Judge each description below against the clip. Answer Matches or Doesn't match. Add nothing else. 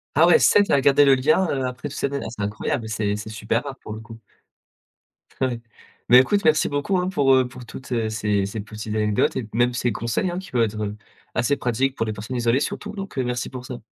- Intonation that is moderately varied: Matches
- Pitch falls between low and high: Doesn't match